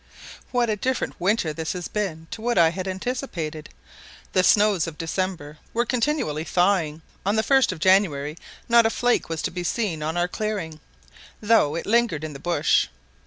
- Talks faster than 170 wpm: Yes, average, 180 wpm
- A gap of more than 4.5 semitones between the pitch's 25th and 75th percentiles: Yes, wide, 5.5 semitones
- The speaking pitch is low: No, medium, 185 Hz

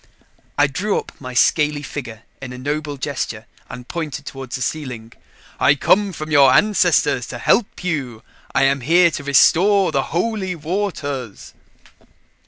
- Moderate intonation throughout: Yes, average, 4.8 semitones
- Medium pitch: Yes, medium, 145 Hz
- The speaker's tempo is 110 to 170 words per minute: Yes, average, 150 wpm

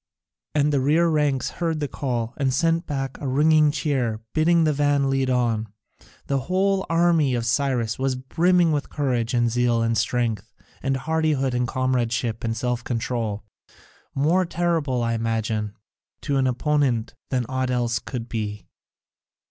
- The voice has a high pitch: No, low, 130 Hz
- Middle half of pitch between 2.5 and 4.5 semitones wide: Yes, average, 4.0 semitones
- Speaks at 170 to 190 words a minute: No, average, 155 wpm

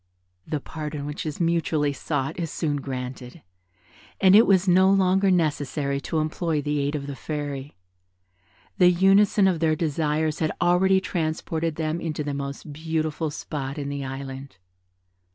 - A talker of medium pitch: Yes, medium, 155 Hz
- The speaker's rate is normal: Yes, average, 155 wpm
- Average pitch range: Yes, average, 3.1 semitones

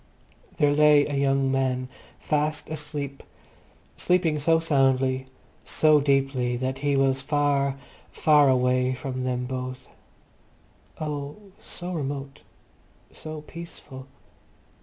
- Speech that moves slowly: Yes, slow, 100 wpm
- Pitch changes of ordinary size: No, narrow, 2.3 semitones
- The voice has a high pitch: No, medium, 140 Hz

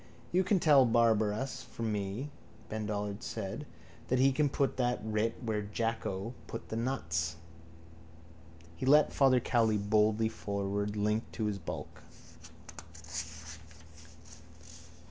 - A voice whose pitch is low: Yes, low, 110 Hz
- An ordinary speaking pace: No, slow, 120 wpm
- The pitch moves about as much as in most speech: Yes, average, 3.7 semitones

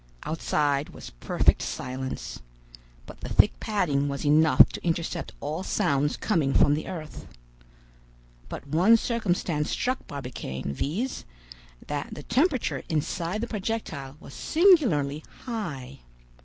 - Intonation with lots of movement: Yes, wide, 7.1 semitones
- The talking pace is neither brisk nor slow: No, slow, 120 wpm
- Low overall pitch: No, medium, 155 Hz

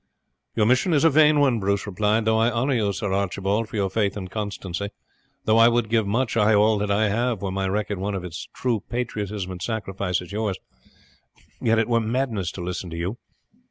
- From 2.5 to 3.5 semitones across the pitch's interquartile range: Yes, average, 2.8 semitones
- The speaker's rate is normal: No, fast, 215 wpm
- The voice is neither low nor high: No, low, 105 Hz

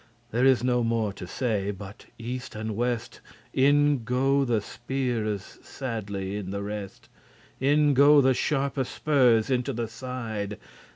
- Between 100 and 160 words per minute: Yes, average, 150 wpm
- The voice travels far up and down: No, average, 3.8 semitones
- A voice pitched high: No, low, 120 Hz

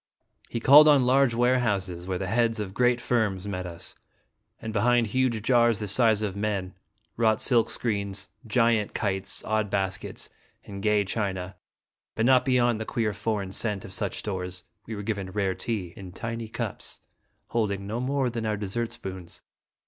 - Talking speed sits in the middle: Yes, average, 170 wpm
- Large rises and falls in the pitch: No, average, 3.3 semitones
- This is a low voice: Yes, low, 110 Hz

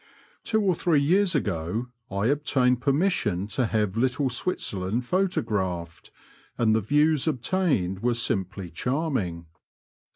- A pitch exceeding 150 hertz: No, low, 125 Hz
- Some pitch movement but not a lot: No, wide, 7.2 semitones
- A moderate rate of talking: No, slow, 120 wpm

